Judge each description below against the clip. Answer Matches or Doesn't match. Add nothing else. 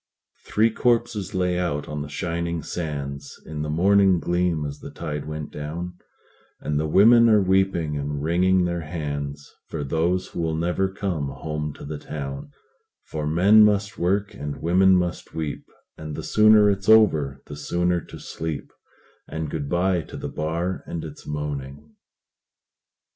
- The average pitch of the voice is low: Matches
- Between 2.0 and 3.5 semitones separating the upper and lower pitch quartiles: Doesn't match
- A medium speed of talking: Matches